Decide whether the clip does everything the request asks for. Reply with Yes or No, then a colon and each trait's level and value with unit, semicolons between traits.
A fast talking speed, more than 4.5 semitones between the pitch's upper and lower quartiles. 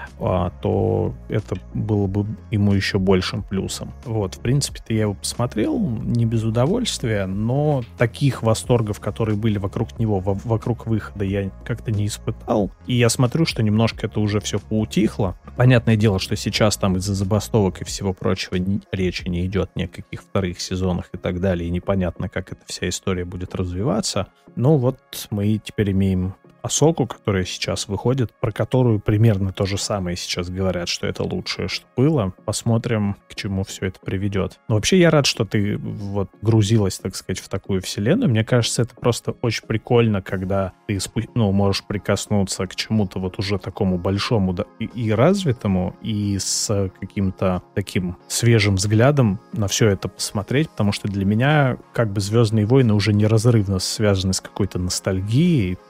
No: fast, 165 wpm; average, 3.1 semitones